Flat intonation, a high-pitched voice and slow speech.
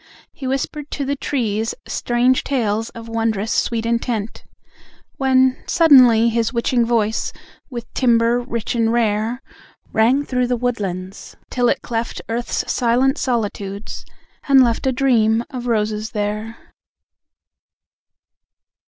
Yes: narrow, 2.3 semitones; high, 235 Hz; slow, 120 wpm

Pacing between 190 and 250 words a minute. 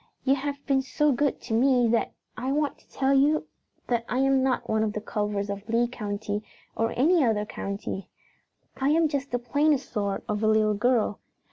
Yes: average, 200 wpm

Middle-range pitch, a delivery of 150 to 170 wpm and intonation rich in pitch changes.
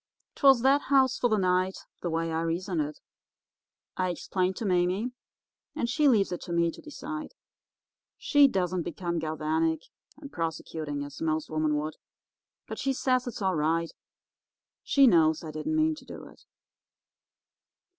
Yes: medium, 180 Hz; average, 155 wpm; wide, 7.5 semitones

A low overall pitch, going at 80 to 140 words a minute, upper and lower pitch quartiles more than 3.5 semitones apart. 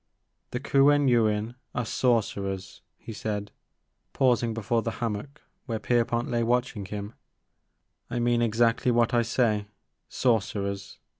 No: low, 115 Hz; slow, 135 wpm; narrow, 2.4 semitones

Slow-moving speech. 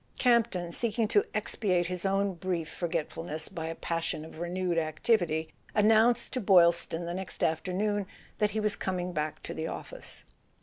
No: average, 180 wpm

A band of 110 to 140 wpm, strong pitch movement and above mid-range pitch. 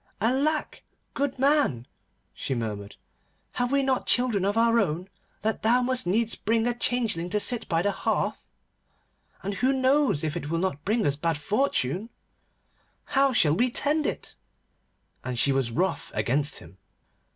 No: average, 160 wpm; wide, 8.9 semitones; high, 210 Hz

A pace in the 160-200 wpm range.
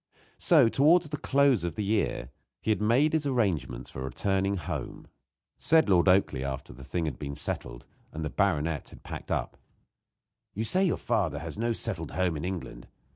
Yes: average, 180 wpm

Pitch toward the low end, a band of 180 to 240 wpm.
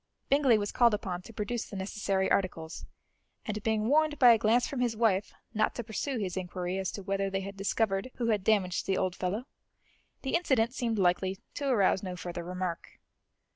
No: high, 205 Hz; average, 195 wpm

